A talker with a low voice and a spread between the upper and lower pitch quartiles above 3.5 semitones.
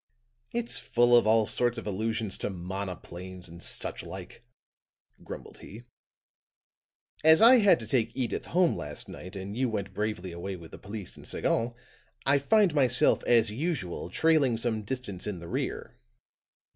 Yes: low, 110 Hz; average, 5.3 semitones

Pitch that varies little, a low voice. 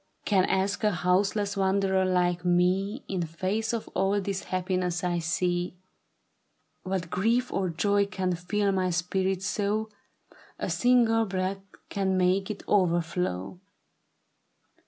No: narrow, 2.0 semitones; high, 190 Hz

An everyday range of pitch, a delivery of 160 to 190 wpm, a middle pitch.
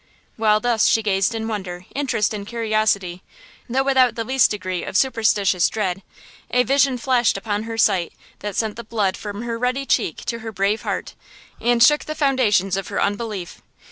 No: average, 3.2 semitones; average, 180 wpm; high, 220 Hz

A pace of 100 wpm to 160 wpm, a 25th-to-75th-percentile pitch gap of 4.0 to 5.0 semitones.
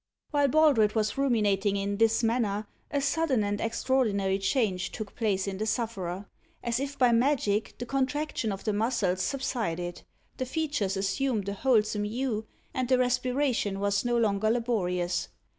Yes: average, 155 wpm; average, 4.3 semitones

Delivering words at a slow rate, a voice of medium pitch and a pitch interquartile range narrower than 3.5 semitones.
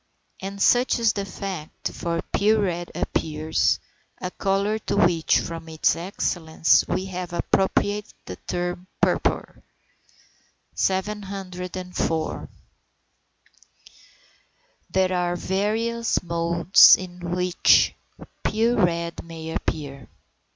Yes: slow, 95 wpm; medium, 180 Hz; average, 2.7 semitones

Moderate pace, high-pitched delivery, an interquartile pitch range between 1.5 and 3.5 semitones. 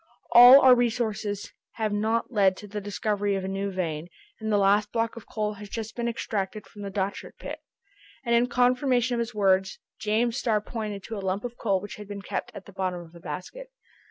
No: fast, 215 wpm; high, 210 Hz; average, 3.0 semitones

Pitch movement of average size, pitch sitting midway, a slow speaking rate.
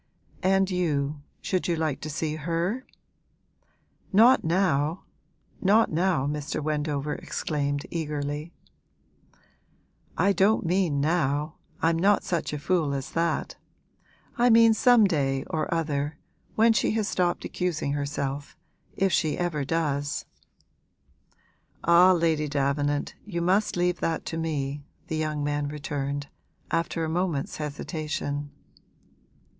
Yes: average, 3.6 semitones; medium, 160 Hz; slow, 120 wpm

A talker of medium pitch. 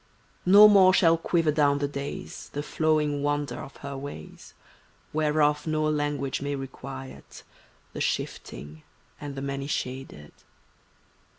Yes: medium, 145 Hz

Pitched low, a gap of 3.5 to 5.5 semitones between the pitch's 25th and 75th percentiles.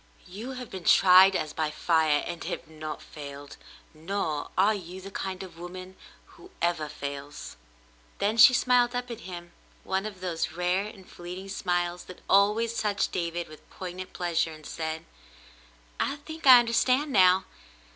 No: medium, 185 Hz; average, 4.0 semitones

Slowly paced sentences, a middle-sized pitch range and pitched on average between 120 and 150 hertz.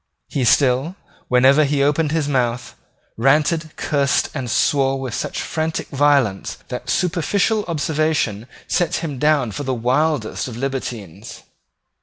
Yes: slow, 130 wpm; average, 3.7 semitones; medium, 140 Hz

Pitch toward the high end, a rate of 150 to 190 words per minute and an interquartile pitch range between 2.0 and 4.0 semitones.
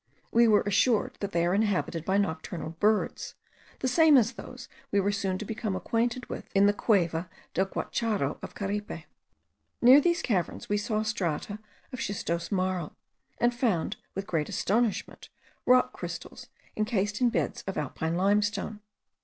Yes: high, 205 Hz; average, 155 wpm; average, 3.5 semitones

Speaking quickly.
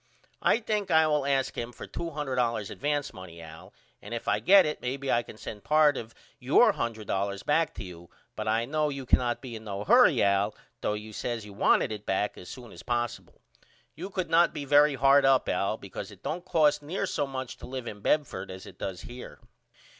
Yes: fast, 220 wpm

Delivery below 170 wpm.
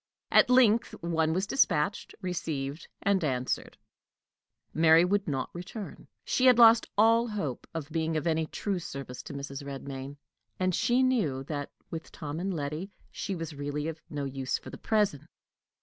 Yes: average, 160 wpm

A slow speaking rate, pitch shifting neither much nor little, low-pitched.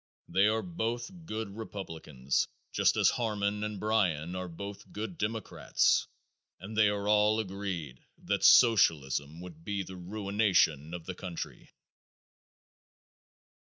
Yes: slow, 125 wpm; average, 3.8 semitones; low, 100 Hz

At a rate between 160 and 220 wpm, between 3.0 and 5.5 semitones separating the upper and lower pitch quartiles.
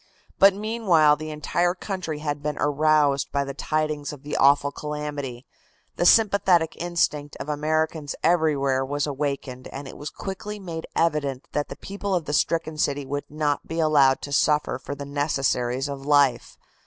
No: average, 165 wpm; narrow, 2.4 semitones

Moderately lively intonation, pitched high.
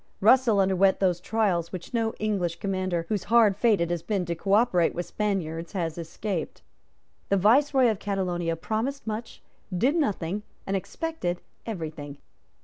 Yes: average, 4.1 semitones; high, 195 Hz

